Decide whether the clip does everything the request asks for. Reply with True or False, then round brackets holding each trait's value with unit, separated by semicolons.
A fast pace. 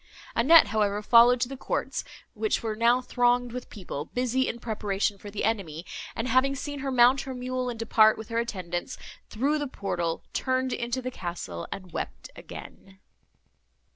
False (170 wpm)